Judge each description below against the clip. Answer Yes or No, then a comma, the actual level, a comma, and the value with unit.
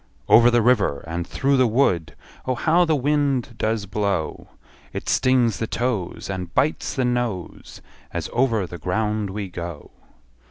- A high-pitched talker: No, low, 115 Hz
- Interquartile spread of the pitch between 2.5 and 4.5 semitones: No, wide, 5.5 semitones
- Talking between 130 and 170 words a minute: Yes, average, 155 wpm